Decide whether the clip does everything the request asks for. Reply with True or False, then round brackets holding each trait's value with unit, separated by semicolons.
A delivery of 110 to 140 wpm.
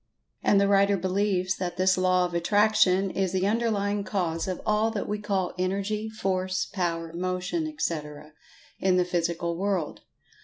False (155 wpm)